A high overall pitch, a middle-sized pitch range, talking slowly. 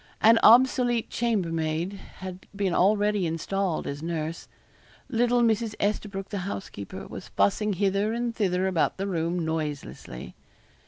Yes: high, 195 Hz; average, 4.5 semitones; slow, 125 wpm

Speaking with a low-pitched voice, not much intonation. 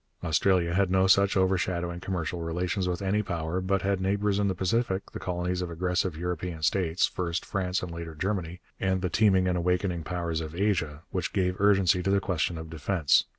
Yes: very low, 90 Hz; narrow, 2.1 semitones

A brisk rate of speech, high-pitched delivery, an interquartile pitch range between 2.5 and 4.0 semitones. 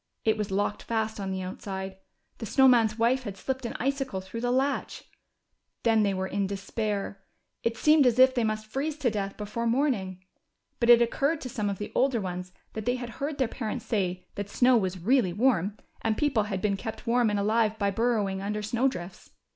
Yes: fast, 210 wpm; high, 220 Hz; average, 3.7 semitones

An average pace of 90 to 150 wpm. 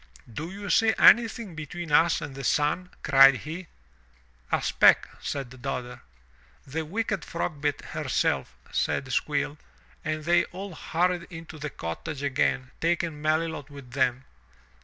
Yes: slow, 135 wpm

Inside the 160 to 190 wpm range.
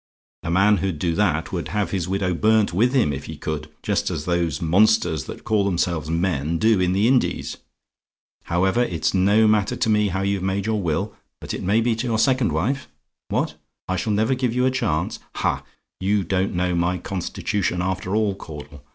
No: average, 200 wpm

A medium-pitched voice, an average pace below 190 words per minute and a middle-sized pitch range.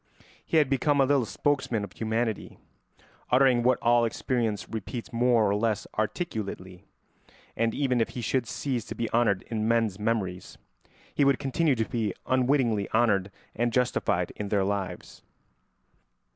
No: low, 115 Hz; average, 150 wpm; average, 3.2 semitones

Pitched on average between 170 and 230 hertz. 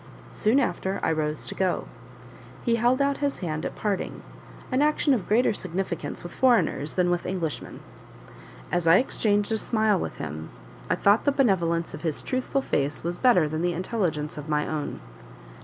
Yes: medium, 185 Hz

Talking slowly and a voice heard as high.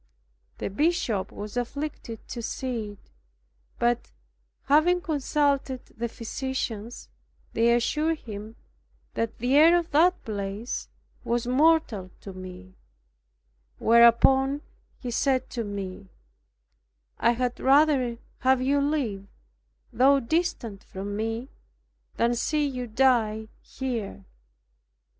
Yes: slow, 105 wpm; high, 240 Hz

